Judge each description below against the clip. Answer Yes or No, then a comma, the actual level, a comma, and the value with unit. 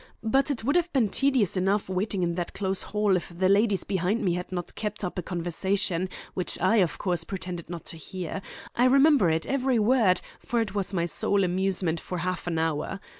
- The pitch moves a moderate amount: Yes, average, 3.4 semitones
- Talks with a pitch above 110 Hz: Yes, high, 190 Hz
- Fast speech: Yes, fast, 210 wpm